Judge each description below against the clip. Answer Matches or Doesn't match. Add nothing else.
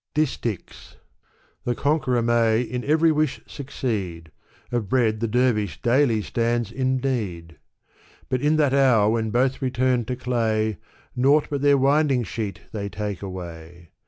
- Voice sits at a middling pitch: Doesn't match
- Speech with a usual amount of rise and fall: Matches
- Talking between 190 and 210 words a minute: Doesn't match